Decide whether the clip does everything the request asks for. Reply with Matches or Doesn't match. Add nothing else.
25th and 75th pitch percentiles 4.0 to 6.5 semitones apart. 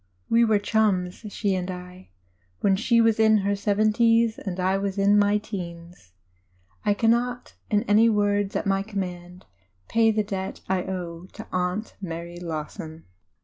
Doesn't match